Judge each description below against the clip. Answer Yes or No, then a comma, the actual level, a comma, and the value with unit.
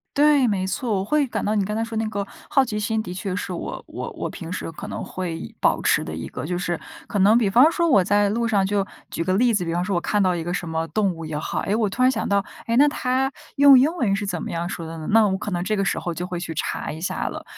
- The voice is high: Yes, high, 200 Hz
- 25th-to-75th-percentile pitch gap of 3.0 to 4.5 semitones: Yes, average, 4.2 semitones